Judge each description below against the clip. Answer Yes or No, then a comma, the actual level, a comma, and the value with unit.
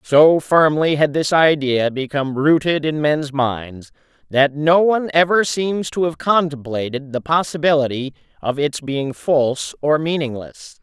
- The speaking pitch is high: No, medium, 150 Hz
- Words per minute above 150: No, average, 145 wpm